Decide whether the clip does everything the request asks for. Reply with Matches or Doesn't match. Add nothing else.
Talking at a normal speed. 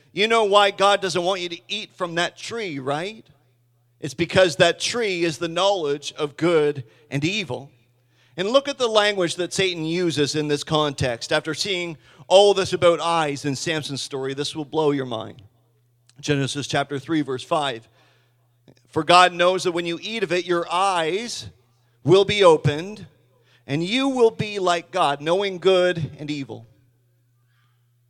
Matches